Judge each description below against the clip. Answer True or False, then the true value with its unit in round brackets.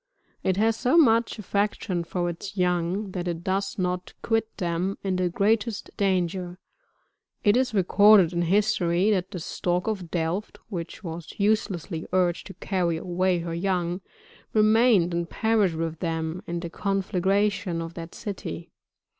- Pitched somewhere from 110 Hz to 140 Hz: False (185 Hz)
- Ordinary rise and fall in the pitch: True (3.0 semitones)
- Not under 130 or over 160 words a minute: True (150 wpm)